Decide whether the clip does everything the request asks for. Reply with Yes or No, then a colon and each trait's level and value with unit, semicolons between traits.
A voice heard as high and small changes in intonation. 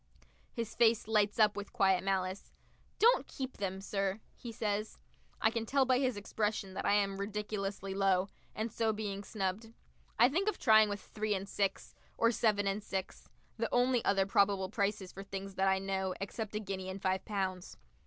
Yes: high, 205 Hz; narrow, 2.2 semitones